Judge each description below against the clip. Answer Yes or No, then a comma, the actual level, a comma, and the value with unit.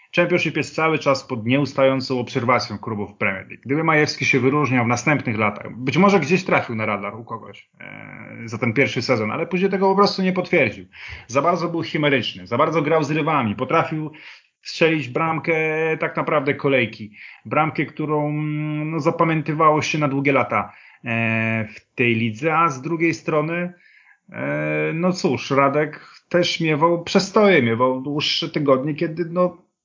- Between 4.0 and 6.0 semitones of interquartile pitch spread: Yes, average, 4.9 semitones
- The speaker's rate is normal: No, fast, 165 wpm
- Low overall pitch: No, medium, 150 Hz